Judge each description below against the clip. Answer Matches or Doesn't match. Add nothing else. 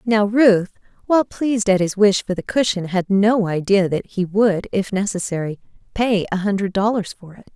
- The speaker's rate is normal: Matches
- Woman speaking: Matches